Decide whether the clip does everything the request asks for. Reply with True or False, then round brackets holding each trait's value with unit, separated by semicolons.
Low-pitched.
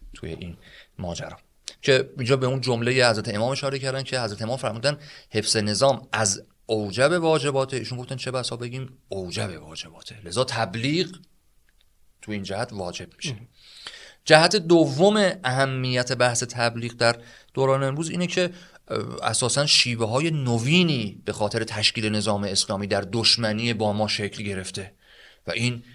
True (120 Hz)